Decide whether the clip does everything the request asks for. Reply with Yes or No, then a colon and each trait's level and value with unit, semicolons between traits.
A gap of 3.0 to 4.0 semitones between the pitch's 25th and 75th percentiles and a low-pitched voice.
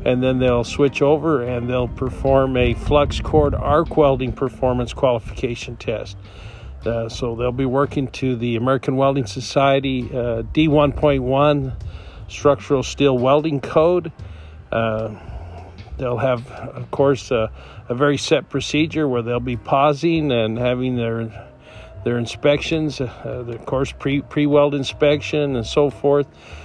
Yes: average, 3.7 semitones; low, 130 Hz